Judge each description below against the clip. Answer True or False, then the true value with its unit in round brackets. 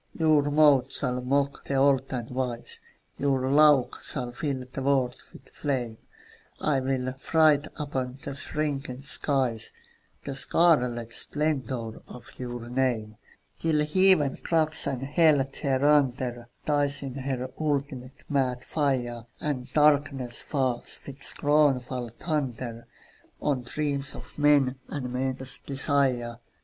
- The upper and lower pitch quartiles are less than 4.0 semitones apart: True (2.5 semitones)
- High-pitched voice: False (135 Hz)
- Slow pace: True (120 wpm)